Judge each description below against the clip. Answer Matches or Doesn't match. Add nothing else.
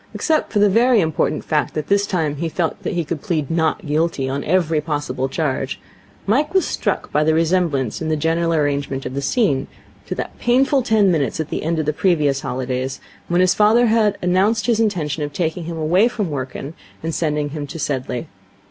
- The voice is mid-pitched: Matches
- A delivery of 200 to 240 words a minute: Matches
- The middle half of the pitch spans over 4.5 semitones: Matches